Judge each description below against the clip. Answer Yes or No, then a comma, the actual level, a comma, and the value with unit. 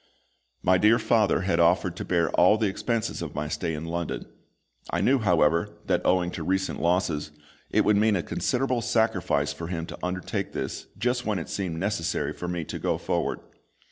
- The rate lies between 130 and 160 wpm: No, average, 190 wpm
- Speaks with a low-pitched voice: Yes, very low, 90 Hz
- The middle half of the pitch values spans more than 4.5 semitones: No, average, 4.1 semitones